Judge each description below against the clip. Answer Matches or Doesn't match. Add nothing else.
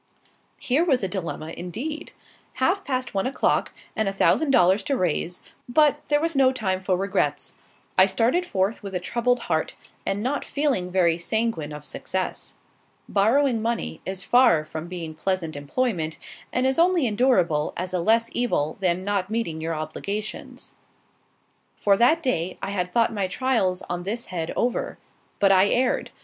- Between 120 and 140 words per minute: Doesn't match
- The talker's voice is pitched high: Matches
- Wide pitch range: Matches